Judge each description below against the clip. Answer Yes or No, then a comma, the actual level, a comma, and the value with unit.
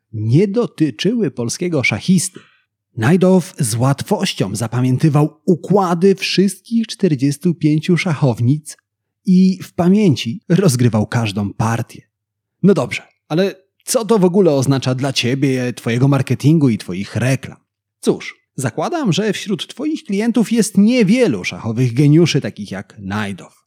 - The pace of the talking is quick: No, average, 115 wpm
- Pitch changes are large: Yes, wide, 7.8 semitones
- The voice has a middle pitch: Yes, medium, 150 Hz